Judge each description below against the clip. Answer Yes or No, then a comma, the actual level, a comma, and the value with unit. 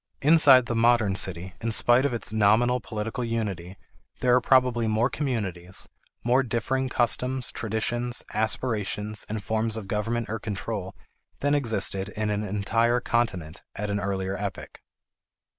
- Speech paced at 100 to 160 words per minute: Yes, average, 140 wpm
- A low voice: Yes, low, 110 Hz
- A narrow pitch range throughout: No, average, 3.0 semitones